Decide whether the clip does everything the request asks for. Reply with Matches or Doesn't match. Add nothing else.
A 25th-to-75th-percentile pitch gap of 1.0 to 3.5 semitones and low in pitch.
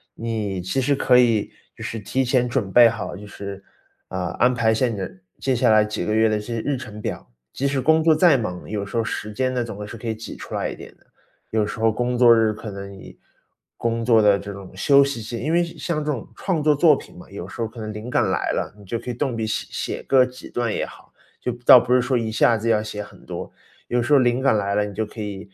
Matches